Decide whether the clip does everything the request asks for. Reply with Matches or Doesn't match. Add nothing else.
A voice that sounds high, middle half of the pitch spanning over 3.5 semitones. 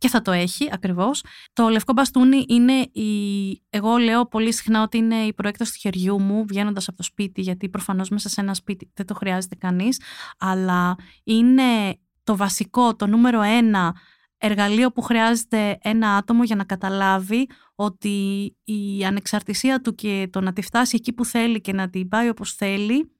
Doesn't match